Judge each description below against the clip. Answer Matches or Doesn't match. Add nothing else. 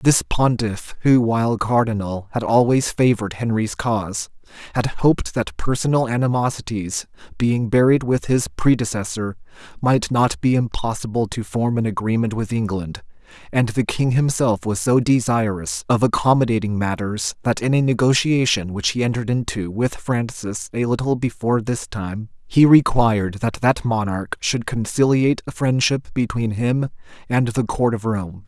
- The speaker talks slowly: Doesn't match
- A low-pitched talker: Matches